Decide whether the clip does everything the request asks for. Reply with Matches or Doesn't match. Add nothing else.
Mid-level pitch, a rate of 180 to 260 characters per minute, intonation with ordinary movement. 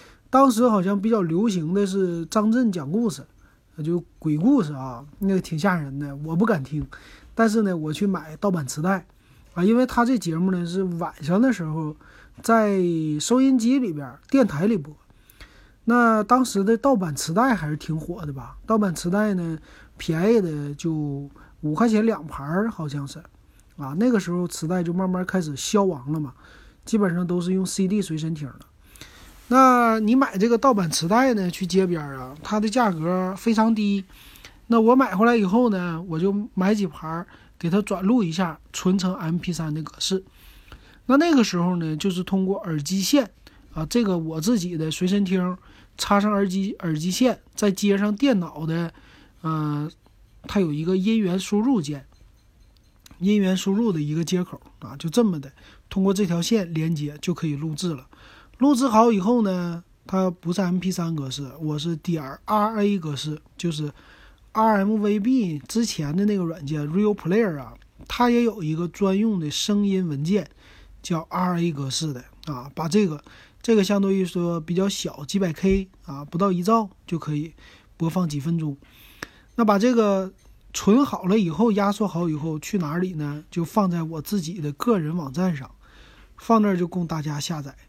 Matches